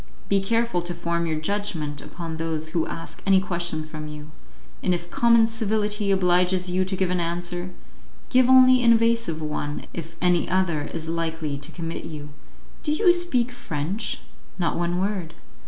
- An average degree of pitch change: Yes, average, 4.2 semitones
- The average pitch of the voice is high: No, medium, 175 Hz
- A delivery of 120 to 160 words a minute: No, average, 170 wpm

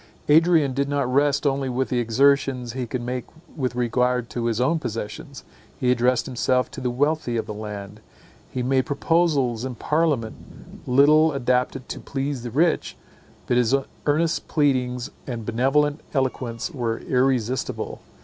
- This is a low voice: Yes, low, 130 Hz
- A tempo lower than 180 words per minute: Yes, average, 150 wpm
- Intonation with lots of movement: No, average, 2.7 semitones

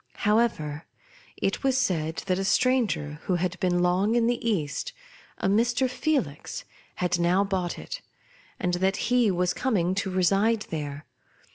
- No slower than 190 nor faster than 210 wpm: No, average, 150 wpm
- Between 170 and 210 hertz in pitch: Yes, high, 190 Hz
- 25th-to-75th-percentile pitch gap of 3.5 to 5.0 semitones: Yes, average, 4.7 semitones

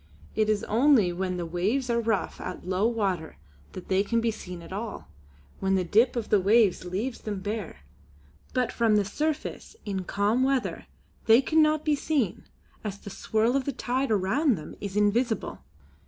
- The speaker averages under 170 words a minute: No, average, 180 wpm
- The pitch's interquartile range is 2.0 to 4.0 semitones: No, average, 4.4 semitones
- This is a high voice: Yes, high, 215 Hz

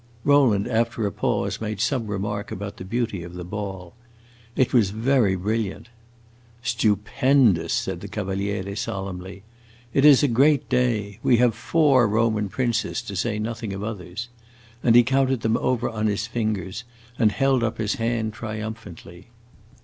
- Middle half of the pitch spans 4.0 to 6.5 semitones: No, average, 3.1 semitones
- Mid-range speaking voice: No, low, 110 Hz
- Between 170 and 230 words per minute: No, average, 155 wpm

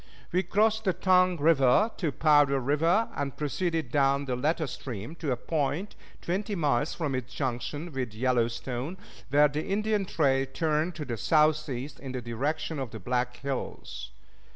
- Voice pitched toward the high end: No, medium, 145 Hz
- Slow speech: No, average, 165 wpm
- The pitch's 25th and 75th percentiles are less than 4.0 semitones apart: No, average, 4.5 semitones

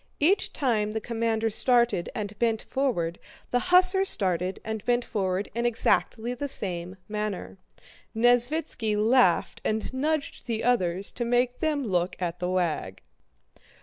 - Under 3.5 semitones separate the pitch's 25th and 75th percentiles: No, average, 4.8 semitones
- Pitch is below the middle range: No, high, 225 Hz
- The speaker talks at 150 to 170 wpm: No, average, 140 wpm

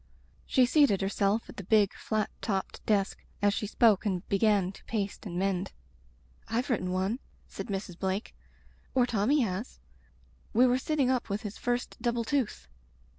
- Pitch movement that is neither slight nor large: Yes, average, 3.7 semitones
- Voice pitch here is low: No, high, 210 Hz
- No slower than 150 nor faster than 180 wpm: Yes, average, 170 wpm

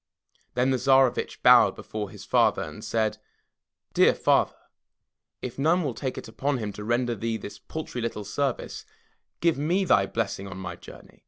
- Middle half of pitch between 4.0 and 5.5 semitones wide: Yes, average, 4.5 semitones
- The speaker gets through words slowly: No, average, 170 wpm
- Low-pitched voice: Yes, low, 120 Hz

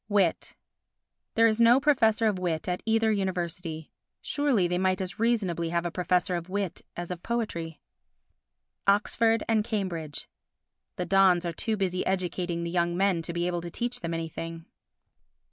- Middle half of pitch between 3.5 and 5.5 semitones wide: Yes, average, 3.9 semitones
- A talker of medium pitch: Yes, medium, 180 Hz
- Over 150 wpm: Yes, average, 160 wpm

